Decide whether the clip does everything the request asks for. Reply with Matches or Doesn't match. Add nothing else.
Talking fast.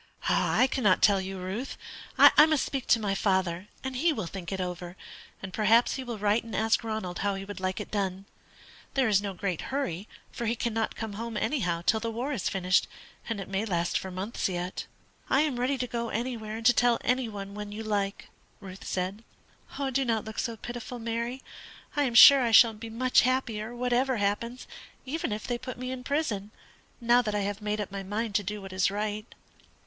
Matches